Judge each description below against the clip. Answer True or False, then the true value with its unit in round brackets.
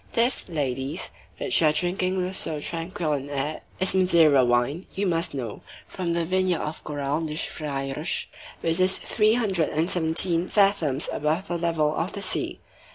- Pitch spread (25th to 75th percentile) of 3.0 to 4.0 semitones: True (3.7 semitones)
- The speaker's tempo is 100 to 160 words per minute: False (170 wpm)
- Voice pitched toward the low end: False (165 Hz)